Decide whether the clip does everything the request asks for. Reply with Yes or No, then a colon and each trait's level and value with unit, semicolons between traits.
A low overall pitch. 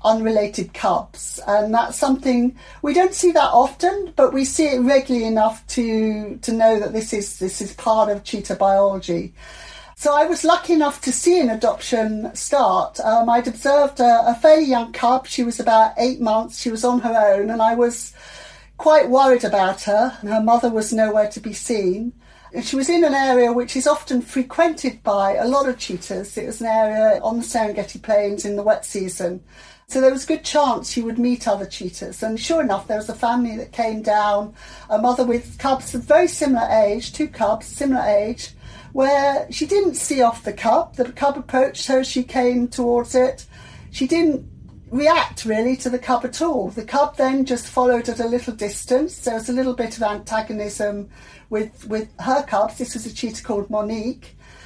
No: high, 240 Hz